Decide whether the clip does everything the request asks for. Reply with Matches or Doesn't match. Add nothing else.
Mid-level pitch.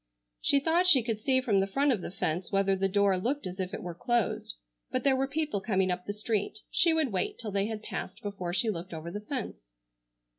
Doesn't match